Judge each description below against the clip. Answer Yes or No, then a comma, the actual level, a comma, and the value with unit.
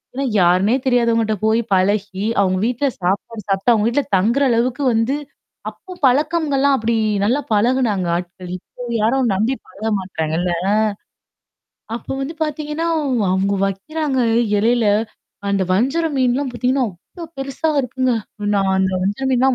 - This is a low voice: No, high, 235 Hz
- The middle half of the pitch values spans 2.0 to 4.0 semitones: No, average, 5.3 semitones